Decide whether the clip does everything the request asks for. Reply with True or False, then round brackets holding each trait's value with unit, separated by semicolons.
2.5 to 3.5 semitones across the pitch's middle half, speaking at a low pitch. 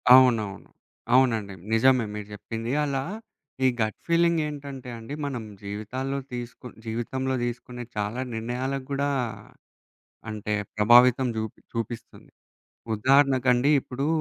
True (3.0 semitones; 125 Hz)